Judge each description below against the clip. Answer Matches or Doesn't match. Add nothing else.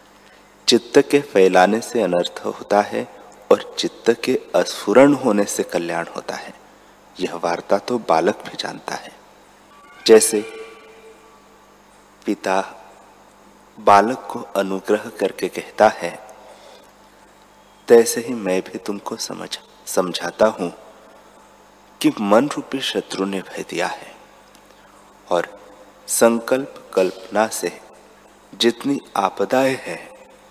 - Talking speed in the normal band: Doesn't match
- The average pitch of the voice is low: Matches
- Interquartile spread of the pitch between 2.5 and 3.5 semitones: Doesn't match